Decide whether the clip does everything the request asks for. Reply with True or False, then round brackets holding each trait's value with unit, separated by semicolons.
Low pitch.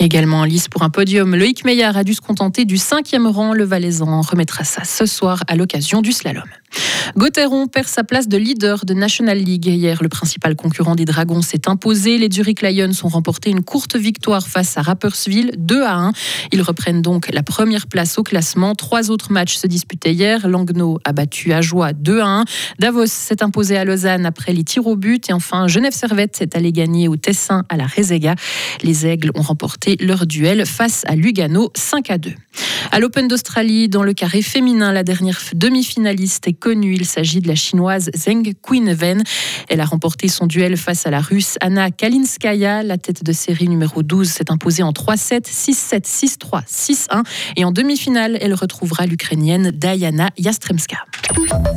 False (190 Hz)